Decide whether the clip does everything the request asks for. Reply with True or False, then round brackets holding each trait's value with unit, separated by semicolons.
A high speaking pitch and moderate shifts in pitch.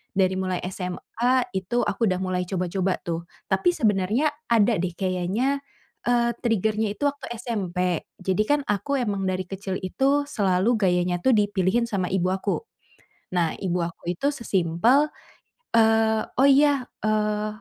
True (200 Hz; 4.0 semitones)